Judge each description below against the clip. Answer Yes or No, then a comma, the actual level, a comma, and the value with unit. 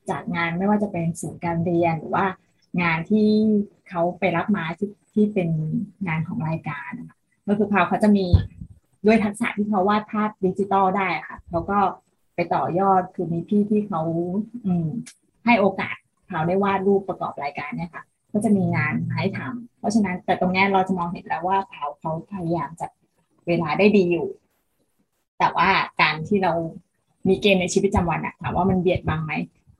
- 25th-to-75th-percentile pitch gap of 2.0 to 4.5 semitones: Yes, average, 3.3 semitones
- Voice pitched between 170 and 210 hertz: Yes, medium, 185 Hz